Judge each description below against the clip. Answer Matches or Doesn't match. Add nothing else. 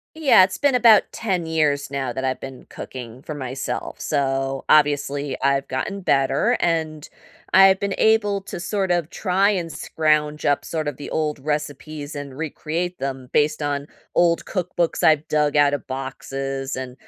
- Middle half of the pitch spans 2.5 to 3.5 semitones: Doesn't match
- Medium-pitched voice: Matches